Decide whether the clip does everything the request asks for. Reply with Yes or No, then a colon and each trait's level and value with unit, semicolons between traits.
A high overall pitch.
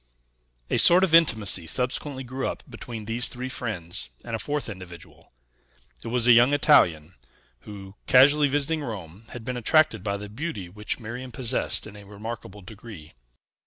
No: low, 115 Hz